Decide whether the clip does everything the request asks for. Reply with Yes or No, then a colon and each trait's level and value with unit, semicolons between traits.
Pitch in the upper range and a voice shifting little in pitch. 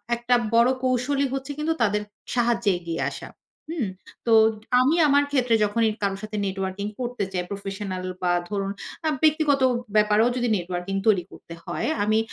No: high, 215 Hz; average, 4.4 semitones